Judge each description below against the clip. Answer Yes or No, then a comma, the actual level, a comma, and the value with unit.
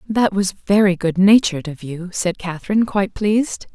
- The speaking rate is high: No, average, 160 wpm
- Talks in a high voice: Yes, high, 195 Hz